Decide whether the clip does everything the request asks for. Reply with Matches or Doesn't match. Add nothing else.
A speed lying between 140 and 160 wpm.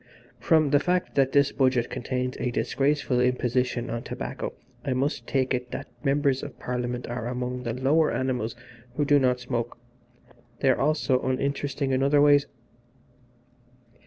Matches